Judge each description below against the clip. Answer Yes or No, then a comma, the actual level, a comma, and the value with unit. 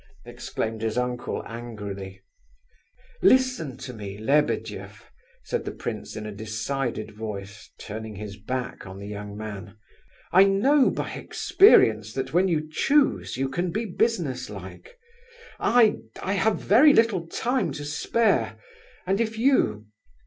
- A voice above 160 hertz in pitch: No, low, 130 Hz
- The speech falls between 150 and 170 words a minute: No, slow, 135 wpm